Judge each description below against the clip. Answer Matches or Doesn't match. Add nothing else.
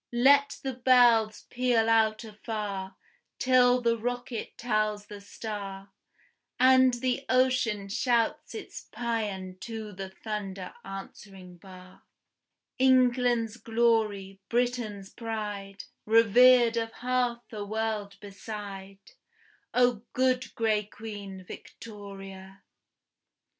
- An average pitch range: Matches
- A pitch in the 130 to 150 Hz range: Doesn't match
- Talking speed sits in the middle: Doesn't match